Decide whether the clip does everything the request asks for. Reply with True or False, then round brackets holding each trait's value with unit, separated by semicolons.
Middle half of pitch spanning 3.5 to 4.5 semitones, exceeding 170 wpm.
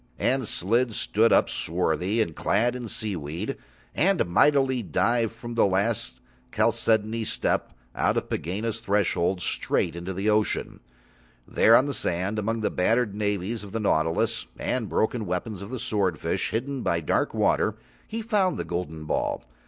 False (4.2 semitones; 150 wpm)